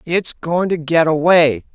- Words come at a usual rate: Yes, average, 170 wpm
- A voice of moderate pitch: Yes, medium, 160 Hz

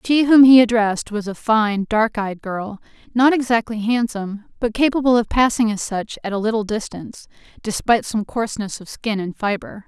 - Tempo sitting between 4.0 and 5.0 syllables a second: No, 5.3 syllables/s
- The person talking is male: No, female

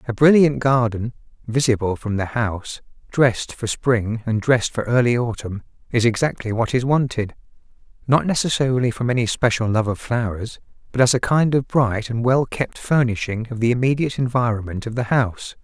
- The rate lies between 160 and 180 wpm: Yes, average, 170 wpm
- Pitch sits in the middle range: No, low, 120 Hz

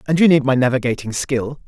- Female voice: No, male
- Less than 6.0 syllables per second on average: No, 6.2 syllables/s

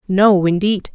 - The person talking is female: Yes, female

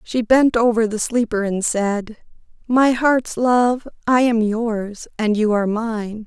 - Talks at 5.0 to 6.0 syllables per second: No, 3.6 syllables/s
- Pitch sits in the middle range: No, high, 225 Hz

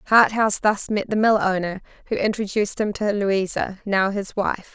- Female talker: Yes, female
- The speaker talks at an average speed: Yes, average, 175 wpm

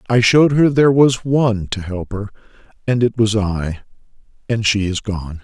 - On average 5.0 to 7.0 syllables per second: Yes, 5.2 syllables/s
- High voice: No, low, 110 Hz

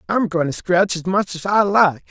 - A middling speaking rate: No, fast, 255 wpm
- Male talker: Yes, male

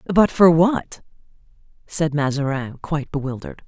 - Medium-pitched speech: Yes, medium, 155 Hz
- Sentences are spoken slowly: Yes, slow, 115 wpm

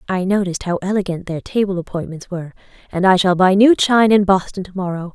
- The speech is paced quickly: Yes, fast, 210 wpm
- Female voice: Yes, female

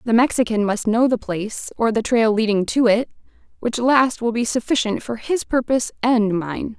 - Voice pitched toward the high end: Yes, high, 230 Hz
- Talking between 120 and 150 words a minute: No, average, 195 wpm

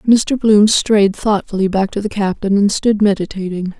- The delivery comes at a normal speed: Yes, average, 175 wpm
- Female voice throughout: Yes, female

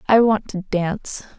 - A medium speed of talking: Yes, average, 175 wpm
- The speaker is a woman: Yes, female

